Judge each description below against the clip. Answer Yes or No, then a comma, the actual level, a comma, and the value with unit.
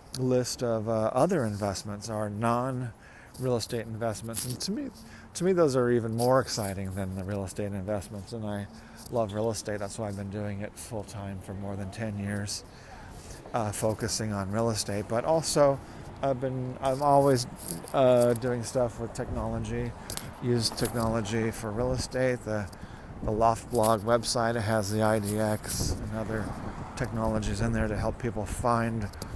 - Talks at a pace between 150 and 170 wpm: Yes, average, 165 wpm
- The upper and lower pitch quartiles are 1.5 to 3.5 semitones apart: Yes, average, 2.7 semitones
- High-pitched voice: No, low, 110 Hz